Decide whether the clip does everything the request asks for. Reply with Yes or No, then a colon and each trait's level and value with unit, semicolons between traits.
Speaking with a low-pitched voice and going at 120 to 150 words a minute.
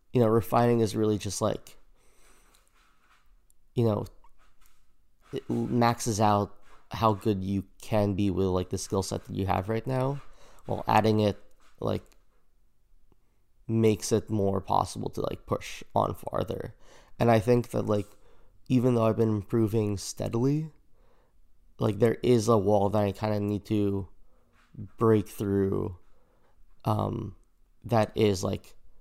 Yes: low, 110 Hz; average, 140 wpm